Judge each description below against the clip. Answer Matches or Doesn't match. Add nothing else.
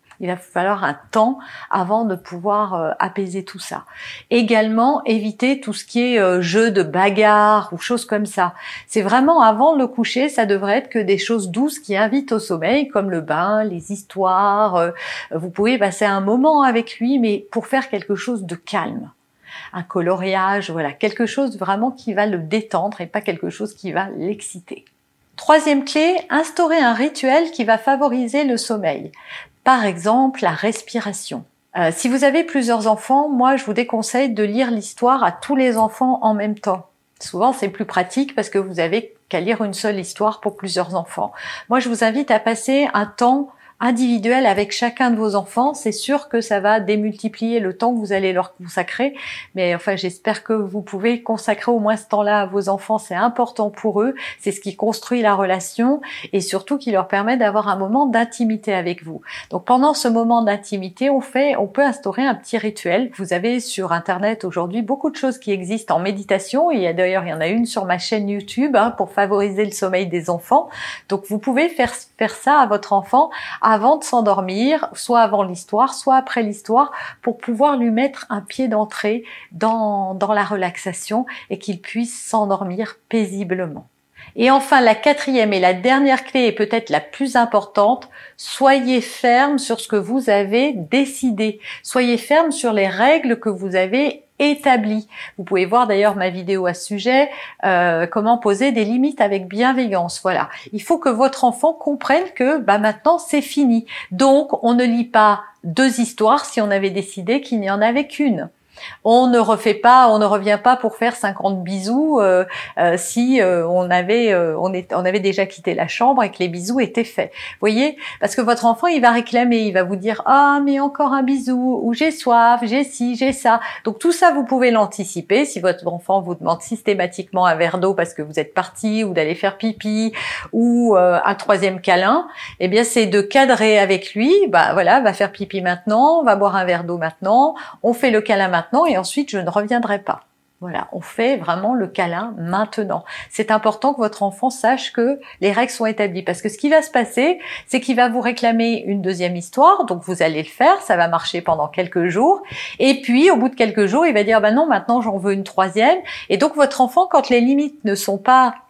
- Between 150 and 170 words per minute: Doesn't match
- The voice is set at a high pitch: Matches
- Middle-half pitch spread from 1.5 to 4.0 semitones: Doesn't match